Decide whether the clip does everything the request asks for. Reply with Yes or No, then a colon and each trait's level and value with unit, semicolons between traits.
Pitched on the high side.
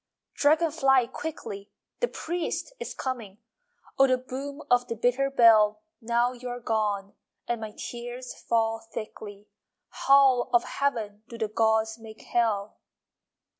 Yes: high, 235 Hz